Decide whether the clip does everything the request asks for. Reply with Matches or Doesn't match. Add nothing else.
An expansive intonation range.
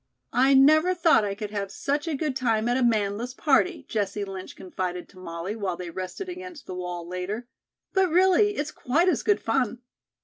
Matches